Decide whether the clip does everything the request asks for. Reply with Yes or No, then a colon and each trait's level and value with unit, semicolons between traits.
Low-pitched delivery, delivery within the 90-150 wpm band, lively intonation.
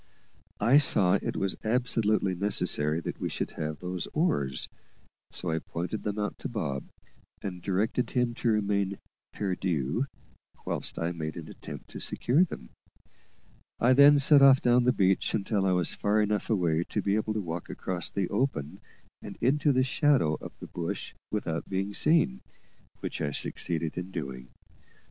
No: low, 100 Hz; average, 165 wpm; wide, 5.9 semitones